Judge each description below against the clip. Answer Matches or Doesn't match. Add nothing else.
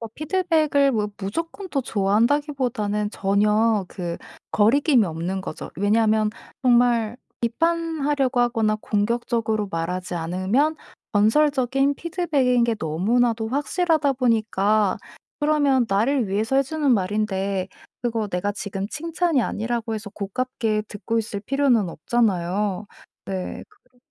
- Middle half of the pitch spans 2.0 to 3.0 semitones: Doesn't match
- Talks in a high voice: Matches